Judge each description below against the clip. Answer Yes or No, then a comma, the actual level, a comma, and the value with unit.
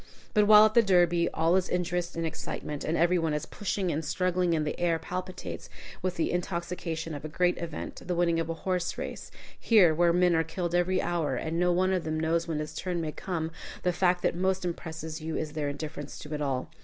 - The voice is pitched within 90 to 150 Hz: No, medium, 170 Hz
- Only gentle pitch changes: Yes, narrow, 2.1 semitones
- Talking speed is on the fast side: Yes, fast, 230 wpm